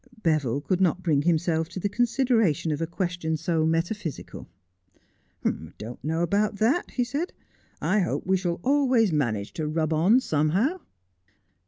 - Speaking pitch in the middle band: Yes, medium, 175 Hz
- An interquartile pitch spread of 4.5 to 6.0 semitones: Yes, average, 5.2 semitones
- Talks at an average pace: Yes, average, 165 wpm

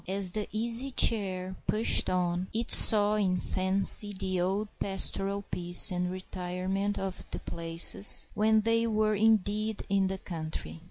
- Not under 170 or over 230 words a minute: No, average, 145 wpm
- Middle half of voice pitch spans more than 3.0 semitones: No, narrow, 2.6 semitones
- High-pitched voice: Yes, high, 195 Hz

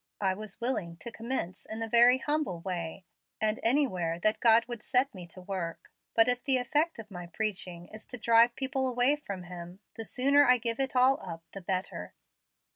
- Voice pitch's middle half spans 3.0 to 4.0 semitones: No, average, 5.3 semitones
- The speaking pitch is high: Yes, high, 225 Hz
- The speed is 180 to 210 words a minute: Yes, average, 200 wpm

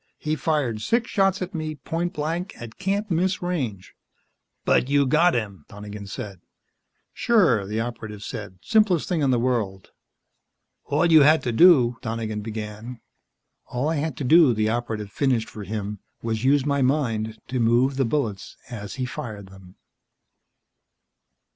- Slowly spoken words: No, average, 160 wpm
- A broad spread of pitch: Yes, wide, 6.3 semitones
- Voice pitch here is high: No, low, 125 Hz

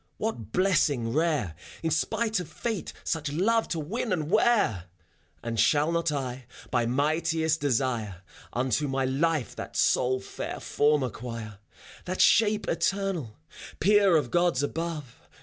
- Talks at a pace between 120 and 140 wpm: Yes, slow, 135 wpm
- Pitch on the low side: No, medium, 150 Hz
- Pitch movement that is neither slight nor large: No, wide, 6.0 semitones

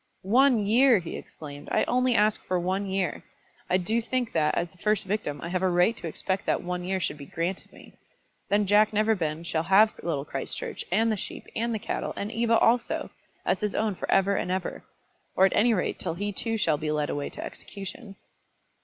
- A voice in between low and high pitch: No, high, 195 Hz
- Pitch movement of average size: Yes, average, 3.9 semitones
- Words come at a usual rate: No, fast, 215 wpm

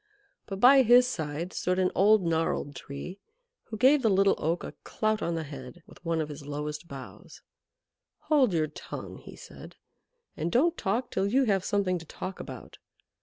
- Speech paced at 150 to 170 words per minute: No, average, 180 wpm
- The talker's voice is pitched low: No, medium, 185 Hz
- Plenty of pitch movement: Yes, wide, 5.8 semitones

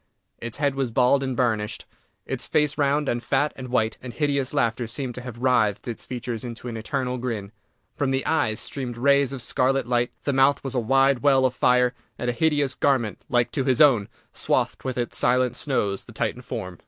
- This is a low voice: Yes, low, 125 Hz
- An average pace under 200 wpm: No, fast, 205 wpm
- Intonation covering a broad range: No, narrow, 2.4 semitones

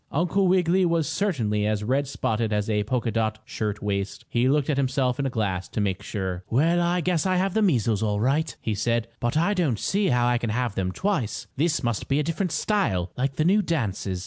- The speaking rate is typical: No, fast, 225 wpm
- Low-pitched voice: Yes, low, 125 Hz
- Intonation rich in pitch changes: Yes, wide, 7.9 semitones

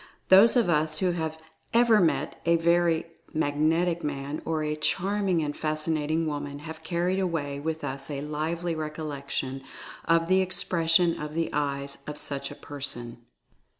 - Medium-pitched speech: Yes, medium, 155 Hz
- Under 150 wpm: No, average, 155 wpm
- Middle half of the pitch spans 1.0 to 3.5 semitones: Yes, average, 2.8 semitones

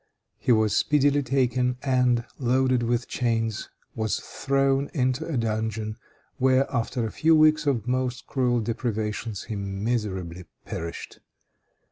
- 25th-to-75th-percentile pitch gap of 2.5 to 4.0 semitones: Yes, average, 3.2 semitones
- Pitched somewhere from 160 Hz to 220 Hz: No, low, 120 Hz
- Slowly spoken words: Yes, slow, 125 wpm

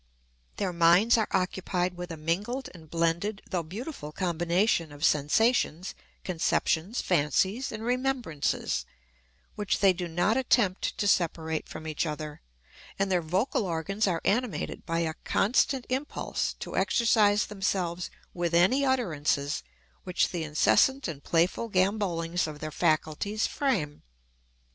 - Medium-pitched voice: Yes, medium, 180 Hz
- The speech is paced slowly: Yes, slow, 130 wpm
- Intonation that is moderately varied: Yes, average, 4.6 semitones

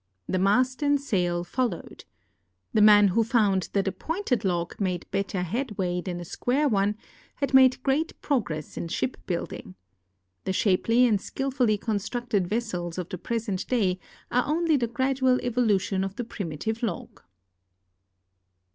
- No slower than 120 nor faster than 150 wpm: Yes, average, 145 wpm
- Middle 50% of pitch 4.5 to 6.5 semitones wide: Yes, average, 5.2 semitones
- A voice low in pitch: No, high, 215 Hz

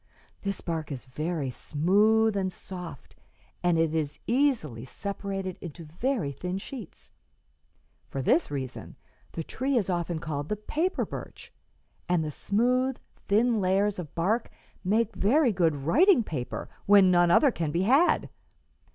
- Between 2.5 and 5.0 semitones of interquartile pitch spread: No, wide, 5.6 semitones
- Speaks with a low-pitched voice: No, medium, 185 Hz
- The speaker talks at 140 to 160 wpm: Yes, average, 145 wpm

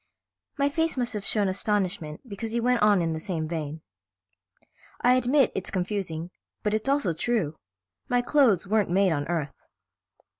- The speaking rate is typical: Yes, average, 160 wpm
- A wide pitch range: Yes, wide, 6.0 semitones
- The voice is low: No, high, 200 Hz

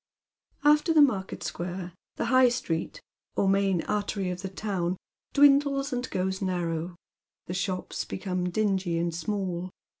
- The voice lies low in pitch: No, high, 190 Hz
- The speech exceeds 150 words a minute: No, average, 140 wpm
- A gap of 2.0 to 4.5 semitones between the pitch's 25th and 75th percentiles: No, average, 4.9 semitones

